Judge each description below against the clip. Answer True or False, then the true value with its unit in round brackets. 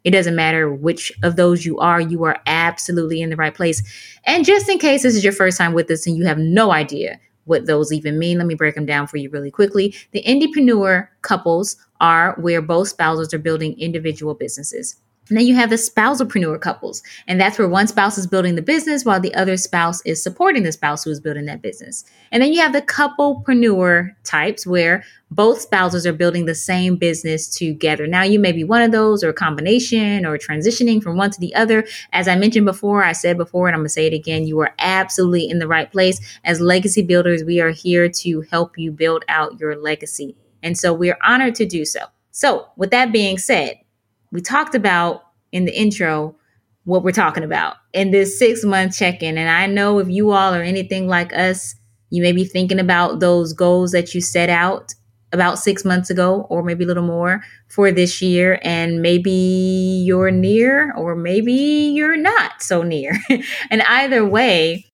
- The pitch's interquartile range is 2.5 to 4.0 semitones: True (3.6 semitones)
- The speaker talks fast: True (210 wpm)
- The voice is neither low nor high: True (180 Hz)